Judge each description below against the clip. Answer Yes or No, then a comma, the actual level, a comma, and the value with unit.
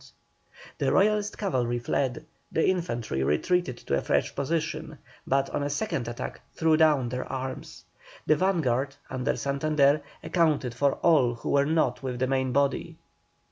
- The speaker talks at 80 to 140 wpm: No, average, 150 wpm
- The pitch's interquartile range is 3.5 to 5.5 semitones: Yes, average, 3.9 semitones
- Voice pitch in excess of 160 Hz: No, medium, 140 Hz